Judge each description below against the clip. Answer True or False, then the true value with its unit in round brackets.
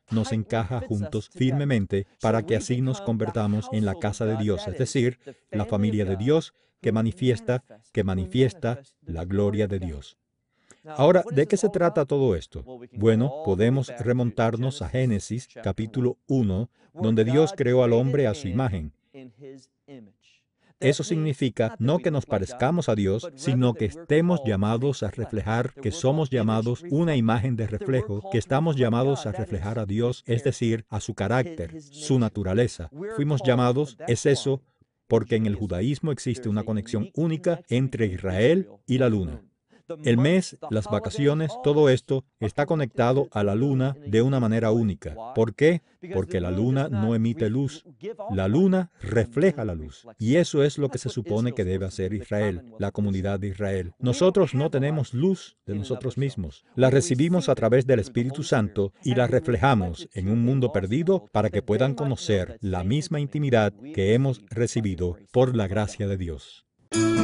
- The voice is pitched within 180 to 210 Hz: False (120 Hz)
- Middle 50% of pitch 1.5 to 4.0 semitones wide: False (4.4 semitones)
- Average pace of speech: True (160 wpm)